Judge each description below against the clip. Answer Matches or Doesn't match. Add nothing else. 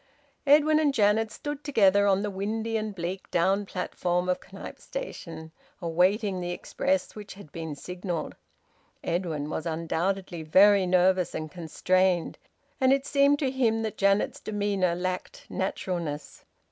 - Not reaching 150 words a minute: Matches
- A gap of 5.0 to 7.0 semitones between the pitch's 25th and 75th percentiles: Doesn't match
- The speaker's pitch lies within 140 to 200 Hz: Matches